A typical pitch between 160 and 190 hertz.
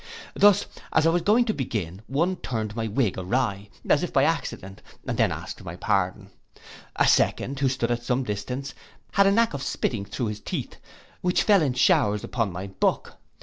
No: low, 125 Hz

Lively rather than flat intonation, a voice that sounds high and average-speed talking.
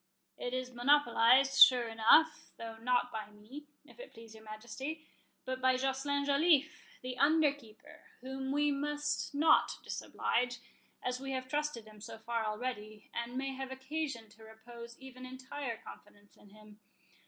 No: average, 3.8 semitones; very high, 255 Hz; average, 155 wpm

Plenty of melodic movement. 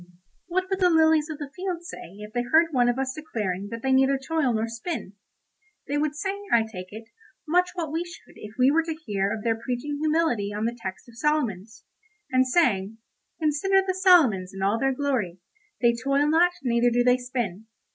Yes: wide, 6.0 semitones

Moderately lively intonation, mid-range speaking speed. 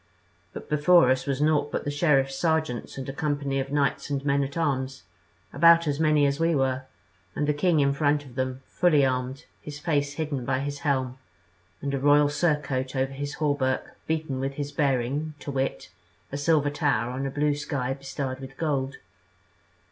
No: narrow, 1.8 semitones; average, 185 wpm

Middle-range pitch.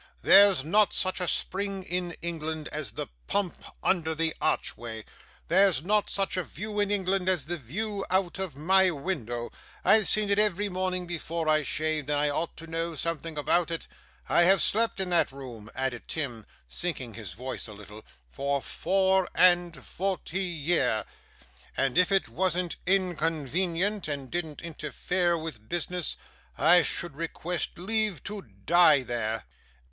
Yes: medium, 170 Hz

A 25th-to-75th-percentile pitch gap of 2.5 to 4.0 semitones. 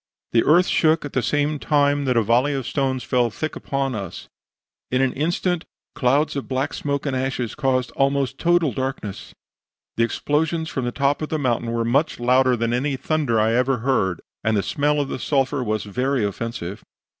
Yes: average, 3.2 semitones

